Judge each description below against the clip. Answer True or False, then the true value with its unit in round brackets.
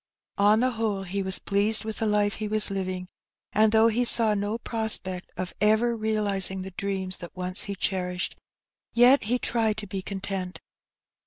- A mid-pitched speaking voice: False (205 Hz)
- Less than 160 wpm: False (175 wpm)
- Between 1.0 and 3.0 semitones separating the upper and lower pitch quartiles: True (2.5 semitones)